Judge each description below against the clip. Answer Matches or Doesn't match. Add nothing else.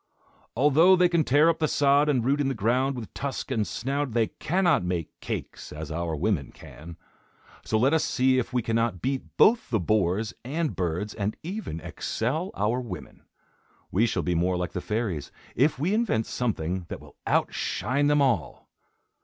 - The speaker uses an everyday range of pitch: Doesn't match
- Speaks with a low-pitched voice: Matches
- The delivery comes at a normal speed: Matches